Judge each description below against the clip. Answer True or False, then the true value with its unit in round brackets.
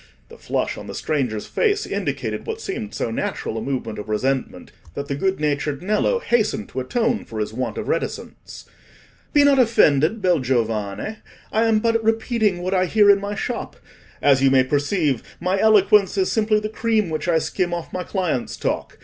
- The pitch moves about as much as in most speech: False (8.2 semitones)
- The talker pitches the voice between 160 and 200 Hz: True (185 Hz)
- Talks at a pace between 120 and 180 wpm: False (190 wpm)